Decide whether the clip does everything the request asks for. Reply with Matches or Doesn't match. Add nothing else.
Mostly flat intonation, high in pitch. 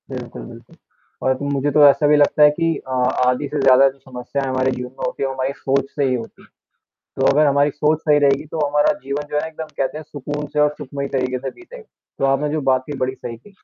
Doesn't match